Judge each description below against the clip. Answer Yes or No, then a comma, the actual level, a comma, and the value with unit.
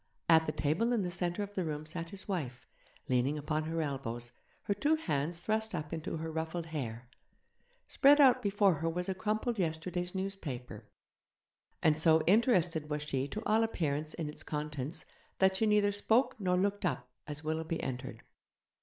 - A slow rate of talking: No, average, 175 wpm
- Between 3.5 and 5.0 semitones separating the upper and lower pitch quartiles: Yes, average, 4.7 semitones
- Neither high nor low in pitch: Yes, medium, 165 Hz